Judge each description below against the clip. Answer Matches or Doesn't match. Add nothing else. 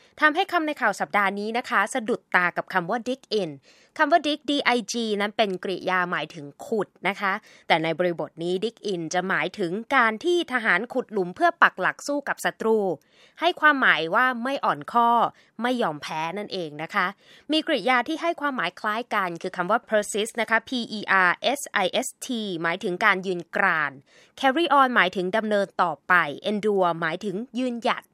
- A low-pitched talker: Doesn't match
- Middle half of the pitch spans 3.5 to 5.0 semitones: Doesn't match